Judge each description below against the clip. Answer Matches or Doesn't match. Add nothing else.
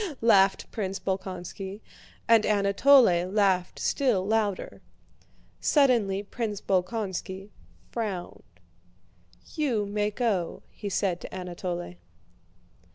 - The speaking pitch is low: Doesn't match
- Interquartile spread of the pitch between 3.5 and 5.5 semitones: Doesn't match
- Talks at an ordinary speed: Doesn't match